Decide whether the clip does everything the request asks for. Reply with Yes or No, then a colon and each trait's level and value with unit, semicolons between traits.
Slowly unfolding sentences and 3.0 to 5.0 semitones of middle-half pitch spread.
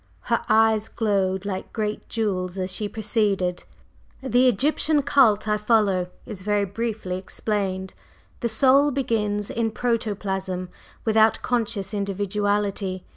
No: slow, 120 wpm; narrow, 2.6 semitones